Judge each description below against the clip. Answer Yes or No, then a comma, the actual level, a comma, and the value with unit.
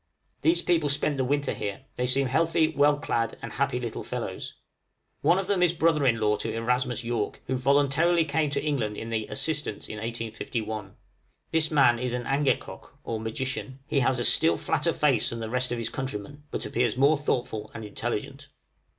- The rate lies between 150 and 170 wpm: No, average, 190 wpm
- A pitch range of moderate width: Yes, average, 4.1 semitones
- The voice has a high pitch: No, low, 130 Hz